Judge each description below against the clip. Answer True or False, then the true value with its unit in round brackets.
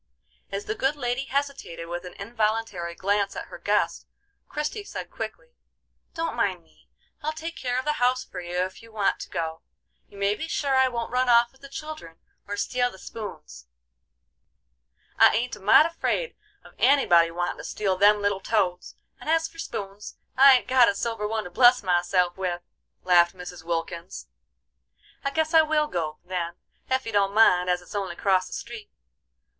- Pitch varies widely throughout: True (6.5 semitones)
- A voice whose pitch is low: False (210 Hz)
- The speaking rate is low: False (185 wpm)